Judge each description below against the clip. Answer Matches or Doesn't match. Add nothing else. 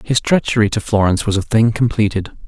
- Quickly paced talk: Doesn't match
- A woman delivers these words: Doesn't match